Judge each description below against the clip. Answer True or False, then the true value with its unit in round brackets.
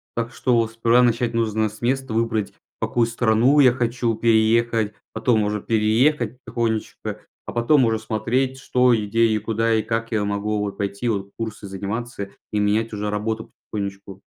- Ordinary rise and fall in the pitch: False (1.9 semitones)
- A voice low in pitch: True (115 Hz)